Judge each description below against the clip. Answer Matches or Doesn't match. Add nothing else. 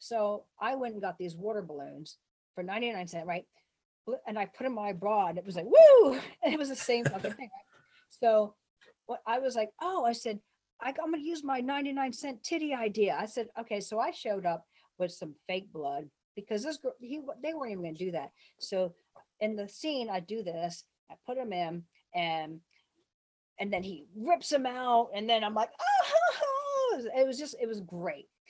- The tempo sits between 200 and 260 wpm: Matches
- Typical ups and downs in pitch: Doesn't match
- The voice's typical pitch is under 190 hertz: Doesn't match